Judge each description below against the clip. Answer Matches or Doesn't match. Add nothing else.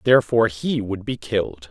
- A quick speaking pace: Doesn't match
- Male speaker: Matches